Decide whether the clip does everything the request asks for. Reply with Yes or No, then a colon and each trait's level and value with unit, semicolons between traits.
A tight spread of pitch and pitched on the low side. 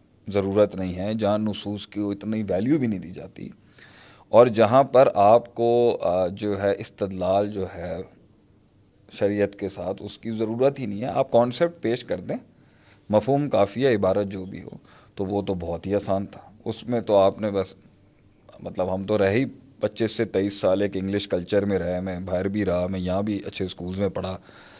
Yes: narrow, 2.3 semitones; low, 100 Hz